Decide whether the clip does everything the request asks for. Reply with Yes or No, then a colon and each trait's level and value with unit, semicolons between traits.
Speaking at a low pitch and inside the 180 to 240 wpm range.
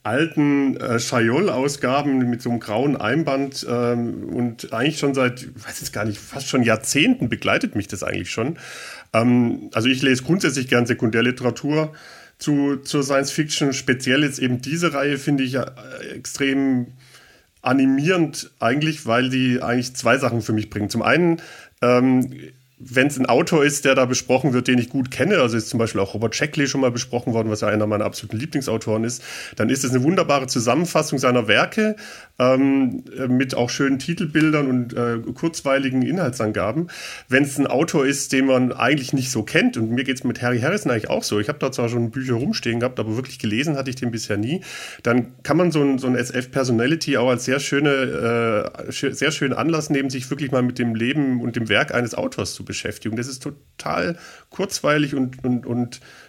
Yes: low, 130 Hz; fast, 190 wpm